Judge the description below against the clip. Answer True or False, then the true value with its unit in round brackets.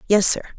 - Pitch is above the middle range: True (205 Hz)